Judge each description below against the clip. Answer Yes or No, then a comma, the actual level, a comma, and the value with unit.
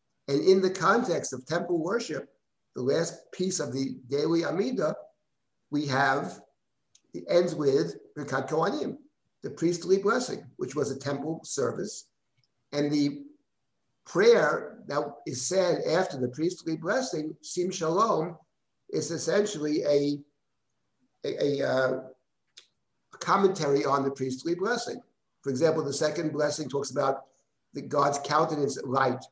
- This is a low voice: No, medium, 150 Hz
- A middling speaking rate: No, slow, 125 wpm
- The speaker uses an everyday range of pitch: Yes, average, 3.7 semitones